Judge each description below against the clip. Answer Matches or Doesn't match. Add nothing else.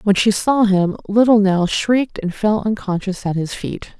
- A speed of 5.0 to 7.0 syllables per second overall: Doesn't match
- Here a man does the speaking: Doesn't match